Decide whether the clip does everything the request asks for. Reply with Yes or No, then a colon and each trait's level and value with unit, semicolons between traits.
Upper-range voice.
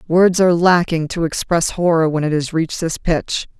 No: medium, 165 Hz